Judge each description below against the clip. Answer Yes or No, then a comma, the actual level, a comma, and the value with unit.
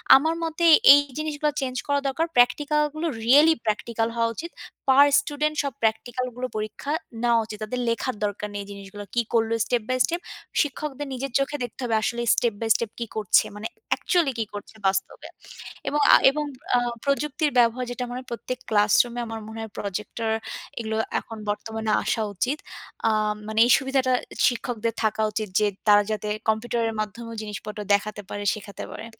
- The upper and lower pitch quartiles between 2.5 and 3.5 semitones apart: No, average, 4.1 semitones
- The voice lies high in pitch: Yes, high, 235 Hz